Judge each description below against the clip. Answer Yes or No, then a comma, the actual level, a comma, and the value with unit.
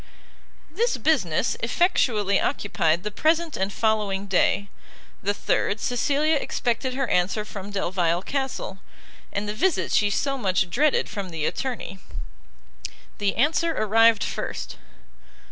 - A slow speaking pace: Yes, slow, 125 wpm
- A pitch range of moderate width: No, wide, 5.9 semitones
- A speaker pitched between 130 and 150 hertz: No, high, 215 Hz